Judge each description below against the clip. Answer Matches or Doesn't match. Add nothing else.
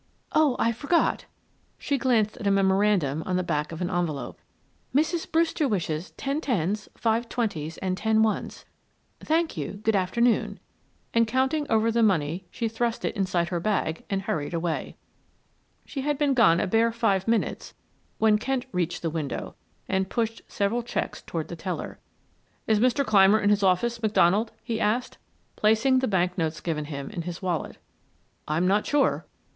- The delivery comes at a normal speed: Matches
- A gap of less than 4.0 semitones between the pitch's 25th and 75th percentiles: Doesn't match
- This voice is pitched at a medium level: Doesn't match